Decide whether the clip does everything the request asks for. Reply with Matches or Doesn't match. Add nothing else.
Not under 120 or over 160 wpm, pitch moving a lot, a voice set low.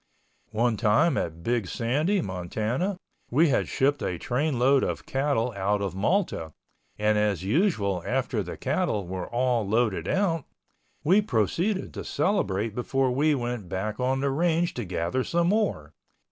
Matches